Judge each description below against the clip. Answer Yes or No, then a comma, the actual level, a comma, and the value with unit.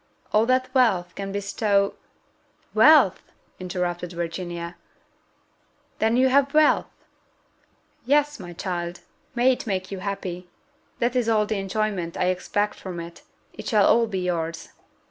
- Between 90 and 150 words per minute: Yes, average, 140 wpm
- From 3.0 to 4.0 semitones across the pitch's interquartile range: No, average, 4.5 semitones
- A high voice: Yes, high, 195 Hz